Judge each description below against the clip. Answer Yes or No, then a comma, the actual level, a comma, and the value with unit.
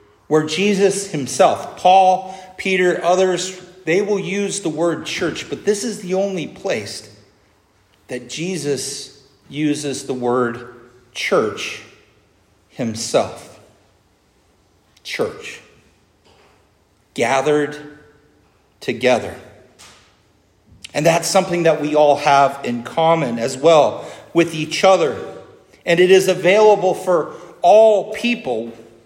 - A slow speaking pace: Yes, slow, 100 wpm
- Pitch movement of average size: No, wide, 8.1 semitones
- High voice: No, medium, 150 Hz